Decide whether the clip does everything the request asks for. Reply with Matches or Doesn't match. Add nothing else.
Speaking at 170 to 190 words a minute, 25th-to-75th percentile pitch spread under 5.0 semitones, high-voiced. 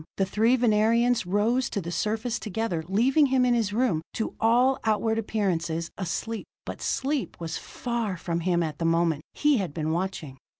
Doesn't match